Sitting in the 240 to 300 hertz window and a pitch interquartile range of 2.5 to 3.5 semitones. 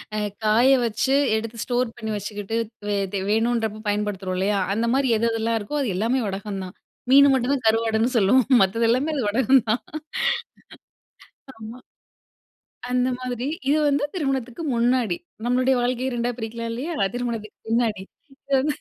No: high, 230 Hz; average, 3.0 semitones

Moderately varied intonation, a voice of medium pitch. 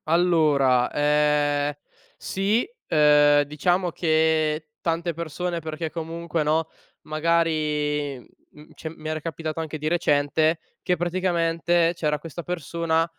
No: narrow, 2.0 semitones; medium, 160 Hz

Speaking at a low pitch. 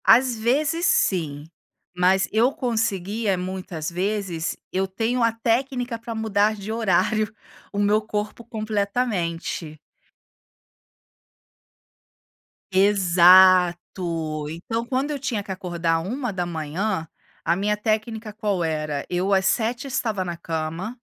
No: high, 200 Hz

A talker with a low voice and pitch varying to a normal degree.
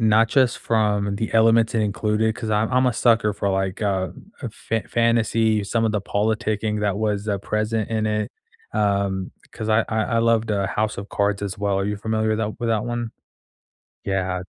No: low, 110 Hz; narrow, 1.8 semitones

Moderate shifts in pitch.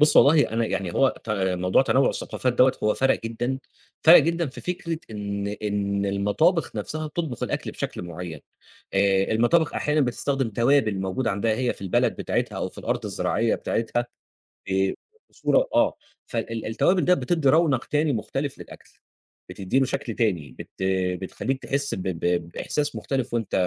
No: wide, 6.0 semitones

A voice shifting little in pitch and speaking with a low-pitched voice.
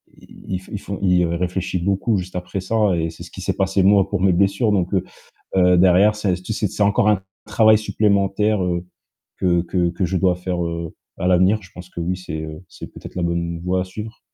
Yes: narrow, 2.2 semitones; very low, 95 Hz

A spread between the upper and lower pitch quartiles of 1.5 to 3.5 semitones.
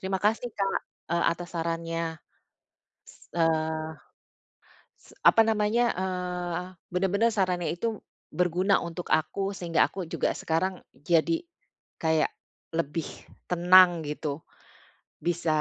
Yes: narrow, 2.5 semitones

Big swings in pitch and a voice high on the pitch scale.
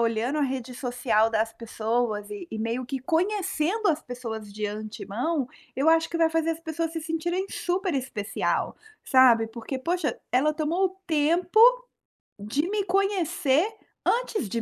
Yes: wide, 6.7 semitones; very high, 285 Hz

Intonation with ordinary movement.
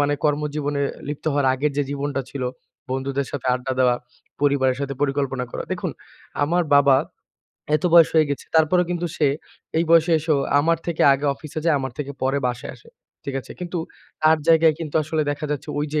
No: narrow, 2.3 semitones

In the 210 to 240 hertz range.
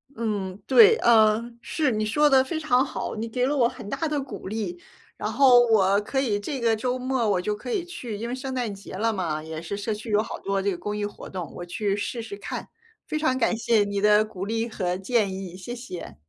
Yes: high, 220 Hz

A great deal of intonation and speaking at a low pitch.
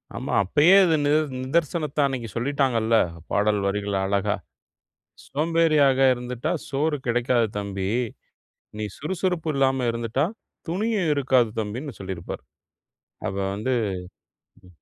Yes: wide, 5.9 semitones; low, 130 Hz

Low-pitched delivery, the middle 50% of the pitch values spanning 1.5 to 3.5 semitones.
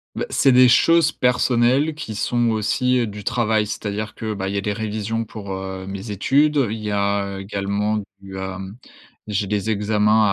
Yes: low, 105 Hz; average, 2.9 semitones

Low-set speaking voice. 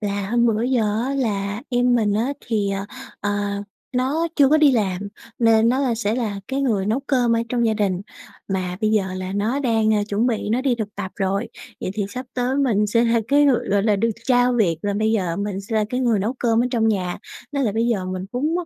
No: high, 220 Hz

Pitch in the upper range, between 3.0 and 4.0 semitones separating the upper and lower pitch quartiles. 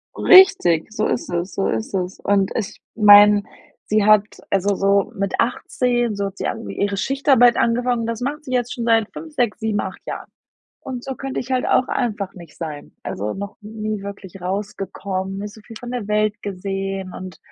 Yes: high, 210 Hz; average, 3.5 semitones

